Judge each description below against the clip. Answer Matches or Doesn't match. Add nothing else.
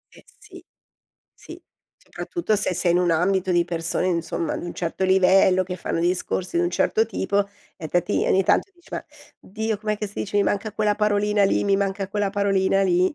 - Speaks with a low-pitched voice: Doesn't match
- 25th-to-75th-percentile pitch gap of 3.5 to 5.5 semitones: Doesn't match